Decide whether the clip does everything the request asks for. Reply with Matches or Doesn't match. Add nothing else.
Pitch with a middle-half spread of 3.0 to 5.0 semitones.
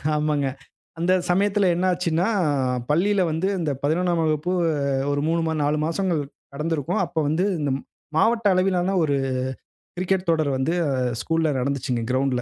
Matches